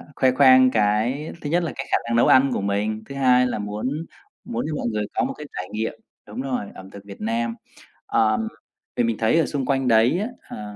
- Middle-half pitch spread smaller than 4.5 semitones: Yes, average, 4.0 semitones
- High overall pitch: No, low, 115 Hz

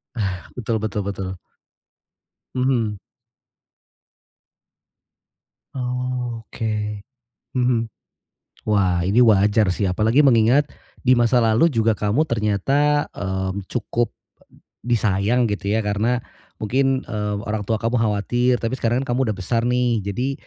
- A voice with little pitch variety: No, average, 3.2 semitones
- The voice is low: Yes, low, 115 Hz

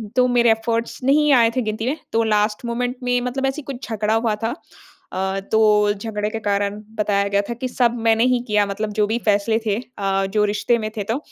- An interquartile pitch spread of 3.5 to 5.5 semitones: No, narrow, 2.5 semitones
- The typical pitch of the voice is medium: No, high, 220 Hz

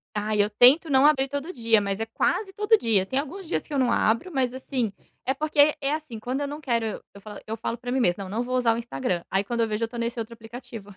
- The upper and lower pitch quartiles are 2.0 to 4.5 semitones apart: Yes, average, 4.1 semitones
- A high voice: Yes, high, 240 Hz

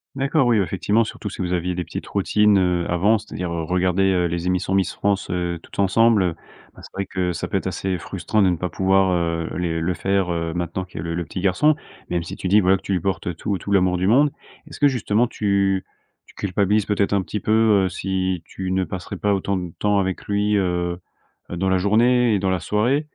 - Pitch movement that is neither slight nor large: No, narrow, 2.3 semitones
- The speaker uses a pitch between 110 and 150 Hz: No, very low, 95 Hz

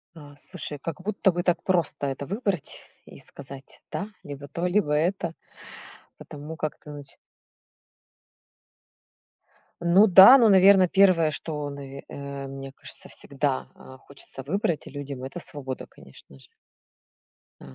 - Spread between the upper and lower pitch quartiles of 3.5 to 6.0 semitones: Yes, average, 4.6 semitones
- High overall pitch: No, medium, 150 Hz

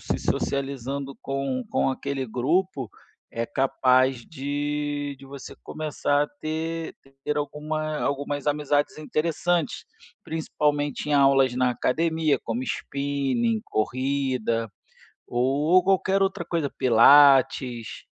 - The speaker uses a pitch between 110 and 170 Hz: Yes, medium, 140 Hz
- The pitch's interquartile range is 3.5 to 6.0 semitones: No, narrow, 2.6 semitones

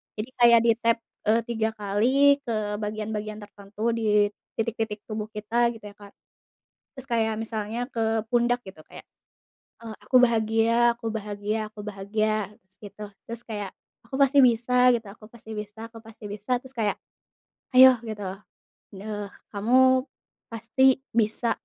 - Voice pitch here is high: Yes, high, 220 Hz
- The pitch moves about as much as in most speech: No, narrow, 2.1 semitones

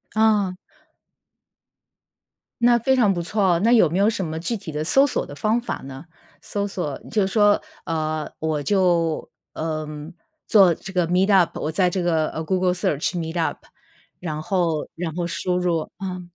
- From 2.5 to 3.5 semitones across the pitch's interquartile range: No, average, 3.9 semitones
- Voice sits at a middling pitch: Yes, medium, 180 Hz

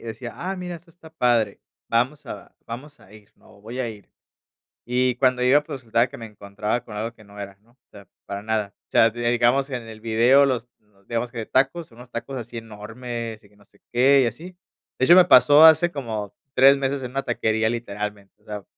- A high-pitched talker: No, low, 120 Hz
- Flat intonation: No, average, 3.6 semitones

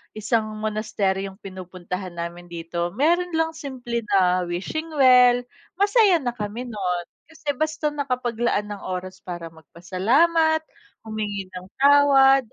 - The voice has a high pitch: Yes, high, 220 Hz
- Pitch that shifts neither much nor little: No, wide, 7.5 semitones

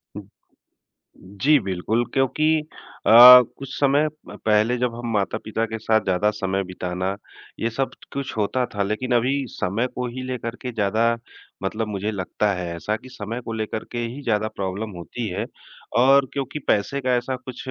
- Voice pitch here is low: Yes, low, 110 Hz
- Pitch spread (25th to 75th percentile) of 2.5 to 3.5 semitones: No, average, 3.9 semitones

